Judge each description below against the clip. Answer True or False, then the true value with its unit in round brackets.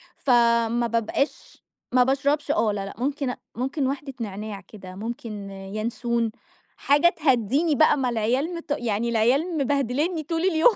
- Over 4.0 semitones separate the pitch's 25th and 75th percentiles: True (4.5 semitones)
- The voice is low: False (245 Hz)